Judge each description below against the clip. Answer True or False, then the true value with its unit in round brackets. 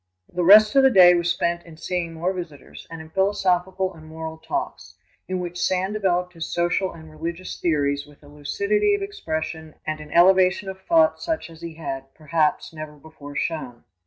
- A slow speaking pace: False (190 wpm)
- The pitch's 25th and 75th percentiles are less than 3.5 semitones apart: True (3.1 semitones)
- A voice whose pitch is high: False (170 Hz)